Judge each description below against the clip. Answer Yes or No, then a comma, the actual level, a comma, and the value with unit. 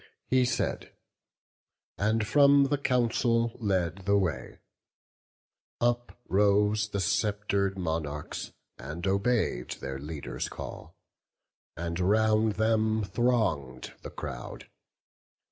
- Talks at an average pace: No, slow, 95 wpm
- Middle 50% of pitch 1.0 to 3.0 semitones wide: No, average, 5.2 semitones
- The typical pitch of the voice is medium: No, low, 105 Hz